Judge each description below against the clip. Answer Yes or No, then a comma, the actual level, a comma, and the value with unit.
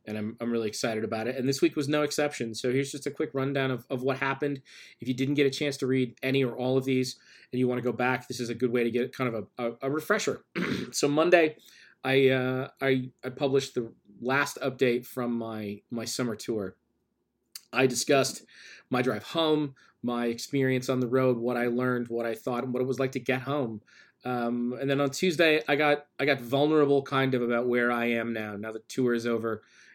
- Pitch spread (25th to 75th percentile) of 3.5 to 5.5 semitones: No, narrow, 2.5 semitones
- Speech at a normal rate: No, fast, 230 wpm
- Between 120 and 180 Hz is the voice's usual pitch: Yes, low, 130 Hz